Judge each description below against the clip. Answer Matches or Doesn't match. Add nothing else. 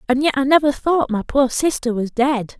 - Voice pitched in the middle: Doesn't match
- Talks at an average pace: Doesn't match